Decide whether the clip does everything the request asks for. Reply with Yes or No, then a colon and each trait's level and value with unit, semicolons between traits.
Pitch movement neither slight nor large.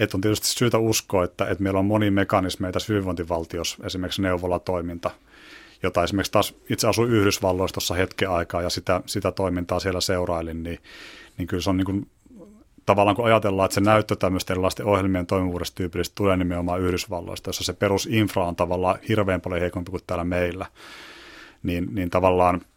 No: narrow, 2.0 semitones